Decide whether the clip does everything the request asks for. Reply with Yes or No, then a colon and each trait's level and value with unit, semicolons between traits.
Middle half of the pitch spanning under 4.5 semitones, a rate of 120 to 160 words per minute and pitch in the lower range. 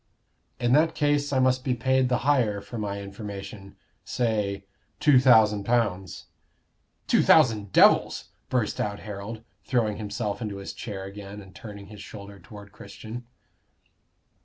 Yes: average, 3.6 semitones; average, 140 wpm; low, 105 Hz